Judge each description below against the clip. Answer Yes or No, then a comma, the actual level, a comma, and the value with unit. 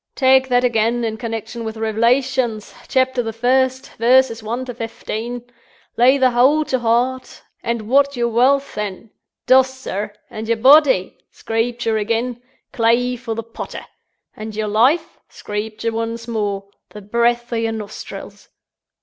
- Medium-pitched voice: No, high, 235 Hz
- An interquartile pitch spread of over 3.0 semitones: No, narrow, 2.4 semitones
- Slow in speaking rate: No, average, 145 wpm